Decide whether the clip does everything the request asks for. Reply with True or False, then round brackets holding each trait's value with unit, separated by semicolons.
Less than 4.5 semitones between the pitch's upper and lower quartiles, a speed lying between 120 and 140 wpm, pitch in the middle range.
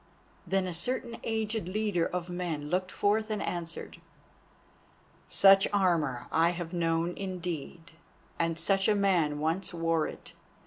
True (2.9 semitones; 135 wpm; 180 Hz)